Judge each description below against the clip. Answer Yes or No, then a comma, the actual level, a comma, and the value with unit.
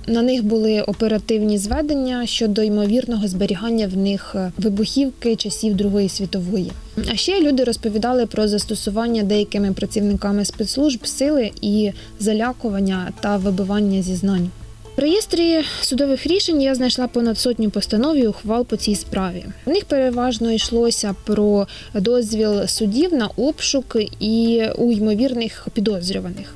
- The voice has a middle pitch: No, high, 220 Hz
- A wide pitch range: No, average, 3.3 semitones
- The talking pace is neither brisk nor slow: Yes, average, 125 wpm